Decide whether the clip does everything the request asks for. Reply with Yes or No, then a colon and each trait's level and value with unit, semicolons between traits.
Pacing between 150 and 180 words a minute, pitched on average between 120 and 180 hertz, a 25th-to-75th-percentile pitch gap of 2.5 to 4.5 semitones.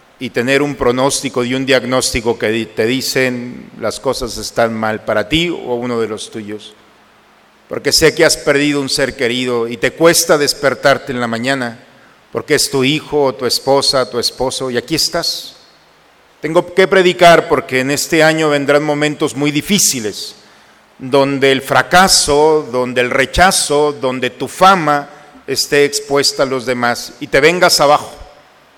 Yes: average, 160 wpm; low, 135 Hz; average, 2.9 semitones